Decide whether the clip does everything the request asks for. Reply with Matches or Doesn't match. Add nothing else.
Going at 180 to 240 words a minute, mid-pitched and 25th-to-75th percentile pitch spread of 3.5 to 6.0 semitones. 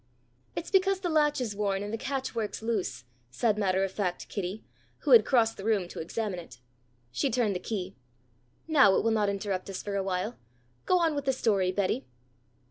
Doesn't match